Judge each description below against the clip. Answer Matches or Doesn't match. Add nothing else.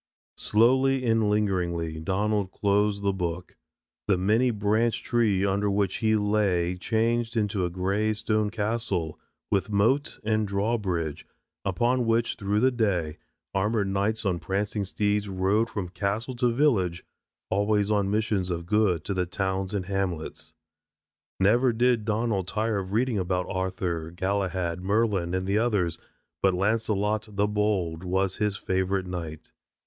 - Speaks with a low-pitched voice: Matches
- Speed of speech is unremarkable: Matches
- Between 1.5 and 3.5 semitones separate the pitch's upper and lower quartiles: Matches